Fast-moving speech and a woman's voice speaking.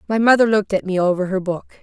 Yes: fast, 260 wpm; female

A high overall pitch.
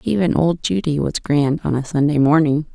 No: medium, 150 Hz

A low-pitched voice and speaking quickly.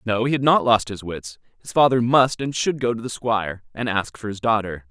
Yes: low, 115 Hz; fast, 255 wpm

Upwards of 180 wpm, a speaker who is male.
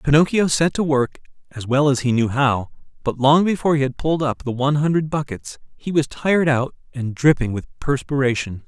Yes: average, 200 wpm; male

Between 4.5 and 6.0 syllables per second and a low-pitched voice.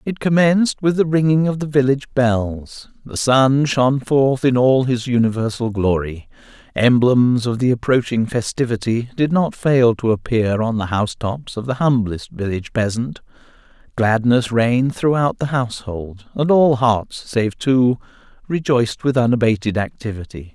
Yes: 4.7 syllables/s; low, 125 Hz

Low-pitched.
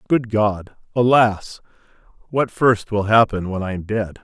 Yes: low, 110 Hz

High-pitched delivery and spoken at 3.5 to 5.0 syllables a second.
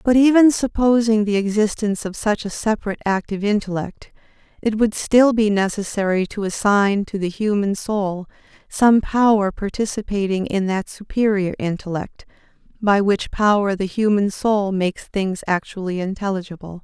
Yes: high, 205 Hz; 4.9 syllables/s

